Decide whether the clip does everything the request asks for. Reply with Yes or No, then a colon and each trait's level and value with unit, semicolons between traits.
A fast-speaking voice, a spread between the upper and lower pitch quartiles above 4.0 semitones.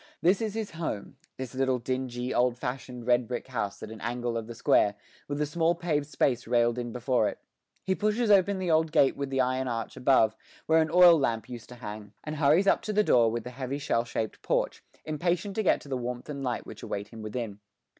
Yes: fast, 230 wpm; average, 5.2 semitones